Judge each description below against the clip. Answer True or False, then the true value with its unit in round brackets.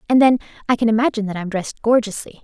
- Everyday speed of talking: False (220 wpm)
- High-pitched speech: True (225 Hz)